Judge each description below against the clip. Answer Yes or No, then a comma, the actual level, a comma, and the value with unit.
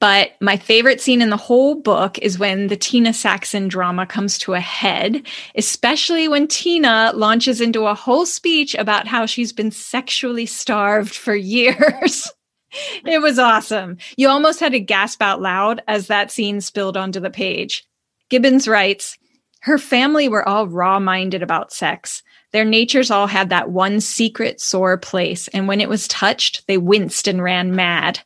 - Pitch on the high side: Yes, high, 215 Hz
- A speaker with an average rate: Yes, average, 170 wpm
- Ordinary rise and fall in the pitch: Yes, average, 4.5 semitones